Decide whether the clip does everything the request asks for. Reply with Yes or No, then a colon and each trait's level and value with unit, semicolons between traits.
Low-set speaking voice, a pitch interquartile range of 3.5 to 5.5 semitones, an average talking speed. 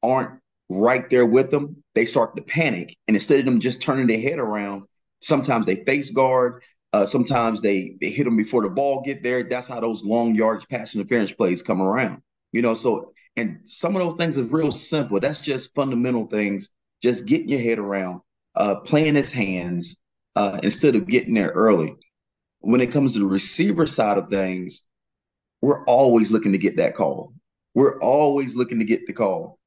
Yes: low, 125 Hz; average, 4.8 semitones; average, 195 wpm